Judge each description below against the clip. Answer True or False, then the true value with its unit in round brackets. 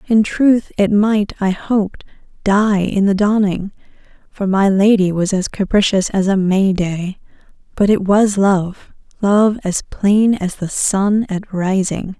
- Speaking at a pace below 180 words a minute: True (150 wpm)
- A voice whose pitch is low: False (200 Hz)